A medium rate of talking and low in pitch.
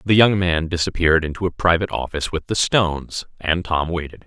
Yes: average, 195 wpm; very low, 85 Hz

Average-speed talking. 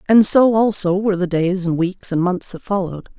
No: fast, 225 wpm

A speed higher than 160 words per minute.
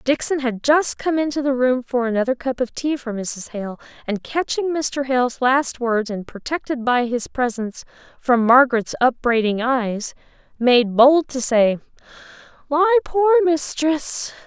No: average, 155 wpm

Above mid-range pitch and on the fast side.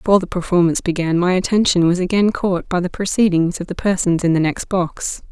No: medium, 180 Hz; fast, 215 wpm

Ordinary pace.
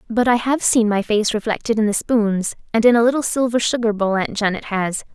No: fast, 235 wpm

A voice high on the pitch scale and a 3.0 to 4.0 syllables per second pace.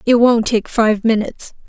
No: high, 225 Hz; 4.8 syllables/s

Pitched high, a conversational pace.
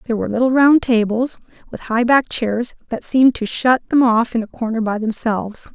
No: high, 235 Hz; fast, 210 wpm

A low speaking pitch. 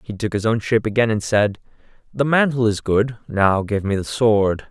Yes: low, 110 Hz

